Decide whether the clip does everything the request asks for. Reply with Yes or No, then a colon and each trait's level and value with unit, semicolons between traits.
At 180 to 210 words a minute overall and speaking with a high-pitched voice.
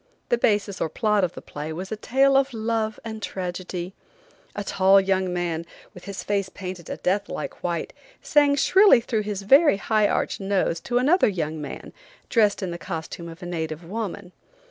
Yes: average, 190 wpm; high, 195 Hz